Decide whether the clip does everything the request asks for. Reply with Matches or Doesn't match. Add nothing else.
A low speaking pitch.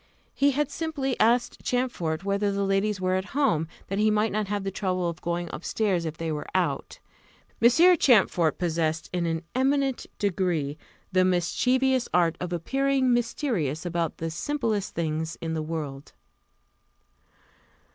Doesn't match